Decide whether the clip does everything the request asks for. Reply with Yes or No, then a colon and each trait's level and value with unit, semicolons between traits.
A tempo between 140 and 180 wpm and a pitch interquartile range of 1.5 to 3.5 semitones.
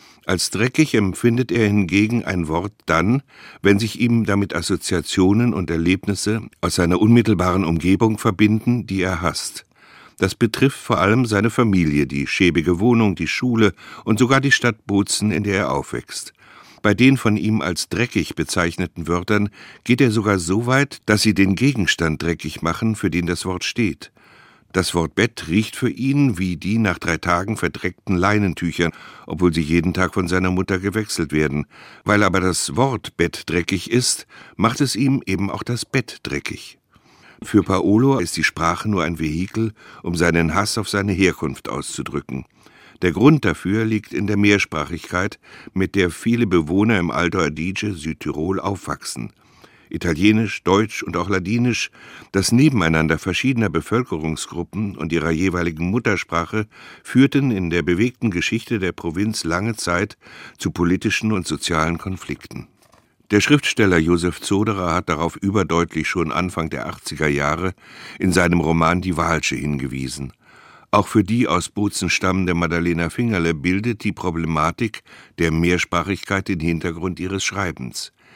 No: average, 150 wpm; average, 4.2 semitones